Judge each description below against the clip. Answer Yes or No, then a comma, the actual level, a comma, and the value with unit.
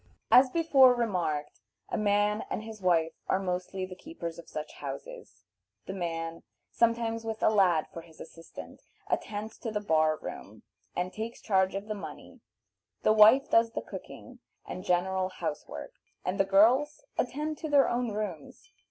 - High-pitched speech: Yes, high, 205 Hz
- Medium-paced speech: Yes, average, 165 wpm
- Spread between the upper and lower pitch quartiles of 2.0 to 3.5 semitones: No, average, 4.4 semitones